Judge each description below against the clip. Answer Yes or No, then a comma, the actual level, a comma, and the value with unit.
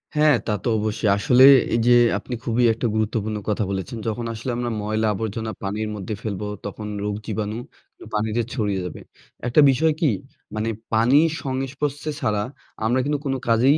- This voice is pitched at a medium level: No, low, 115 Hz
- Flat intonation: No, average, 3.5 semitones